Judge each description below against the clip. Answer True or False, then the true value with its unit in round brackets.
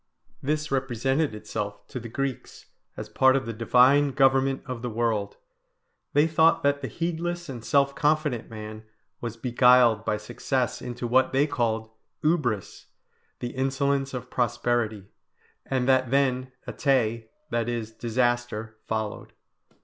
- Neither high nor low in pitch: False (125 Hz)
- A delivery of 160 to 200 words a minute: False (135 wpm)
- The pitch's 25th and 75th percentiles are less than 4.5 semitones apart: True (3.0 semitones)